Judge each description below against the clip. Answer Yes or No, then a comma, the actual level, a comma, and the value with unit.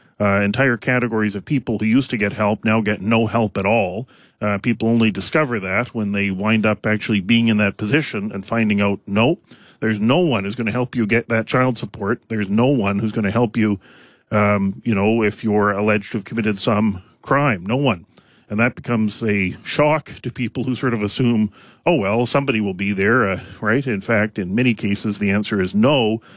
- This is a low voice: Yes, low, 110 Hz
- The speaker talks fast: Yes, fast, 215 wpm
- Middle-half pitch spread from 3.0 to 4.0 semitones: No, narrow, 2.6 semitones